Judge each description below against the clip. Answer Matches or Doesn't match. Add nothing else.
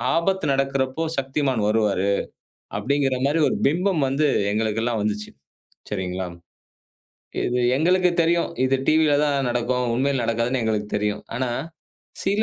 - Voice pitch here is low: Matches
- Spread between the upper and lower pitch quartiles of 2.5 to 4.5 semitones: Doesn't match